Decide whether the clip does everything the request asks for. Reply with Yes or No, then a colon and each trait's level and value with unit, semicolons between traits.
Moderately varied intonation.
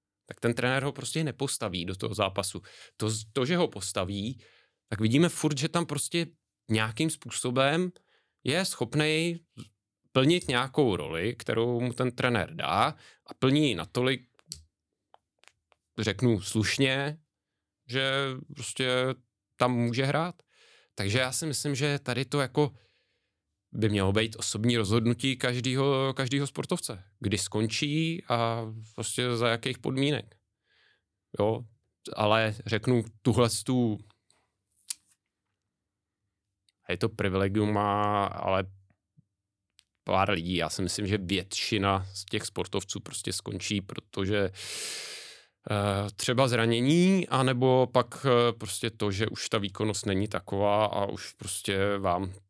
Yes: average, 4.7 semitones